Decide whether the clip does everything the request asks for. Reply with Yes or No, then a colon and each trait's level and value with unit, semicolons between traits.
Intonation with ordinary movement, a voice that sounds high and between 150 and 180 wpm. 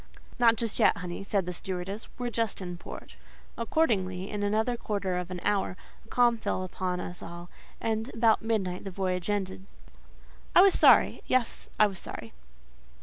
Yes: average, 3.7 semitones; high, 200 Hz; average, 170 wpm